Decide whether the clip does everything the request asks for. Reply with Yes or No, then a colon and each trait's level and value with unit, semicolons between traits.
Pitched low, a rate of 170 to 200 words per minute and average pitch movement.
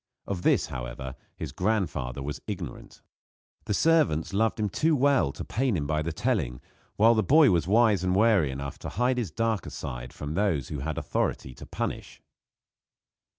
No: very low, 95 Hz; average, 175 wpm; wide, 7.9 semitones